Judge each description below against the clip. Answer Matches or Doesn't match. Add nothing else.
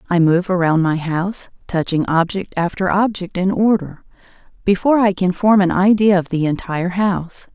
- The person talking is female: Matches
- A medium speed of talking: Matches